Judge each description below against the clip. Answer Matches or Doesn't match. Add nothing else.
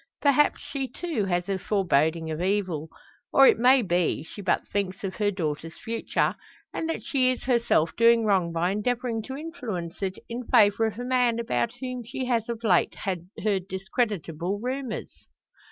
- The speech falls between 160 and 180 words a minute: Matches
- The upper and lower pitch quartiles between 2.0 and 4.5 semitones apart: Doesn't match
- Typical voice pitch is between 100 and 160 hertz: Doesn't match